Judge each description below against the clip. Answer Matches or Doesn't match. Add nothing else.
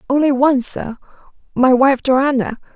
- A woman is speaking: Matches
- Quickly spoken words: Doesn't match